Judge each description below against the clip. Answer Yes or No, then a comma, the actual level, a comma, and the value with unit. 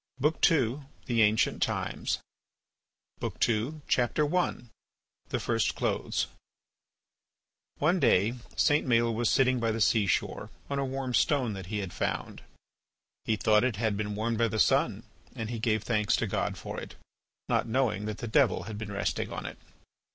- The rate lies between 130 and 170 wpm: Yes, average, 155 wpm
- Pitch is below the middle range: Yes, low, 115 Hz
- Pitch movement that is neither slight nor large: Yes, average, 3.5 semitones